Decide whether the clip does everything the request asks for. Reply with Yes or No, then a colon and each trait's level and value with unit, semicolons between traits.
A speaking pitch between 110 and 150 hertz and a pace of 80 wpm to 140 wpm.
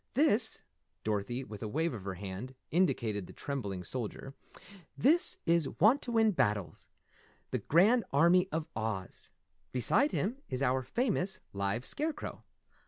Yes: low, 135 Hz; slow, 135 wpm